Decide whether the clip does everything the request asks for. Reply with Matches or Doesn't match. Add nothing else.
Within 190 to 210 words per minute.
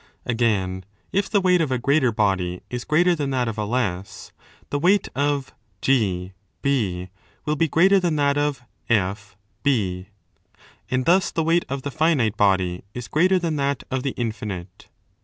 Doesn't match